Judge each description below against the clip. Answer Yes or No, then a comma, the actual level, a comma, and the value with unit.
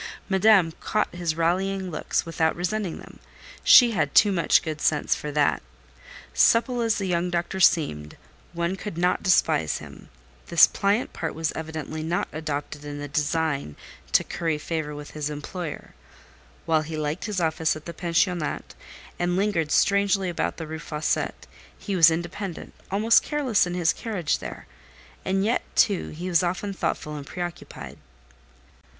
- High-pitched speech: No, medium, 170 Hz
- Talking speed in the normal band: Yes, average, 155 wpm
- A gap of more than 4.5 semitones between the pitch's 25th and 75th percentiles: No, average, 3.7 semitones